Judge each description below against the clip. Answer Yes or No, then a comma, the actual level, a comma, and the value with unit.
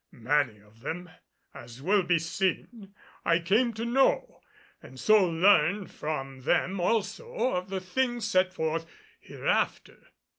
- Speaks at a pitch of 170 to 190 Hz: Yes, medium, 185 Hz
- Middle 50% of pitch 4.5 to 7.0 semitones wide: Yes, average, 5.1 semitones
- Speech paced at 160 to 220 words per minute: No, slow, 135 wpm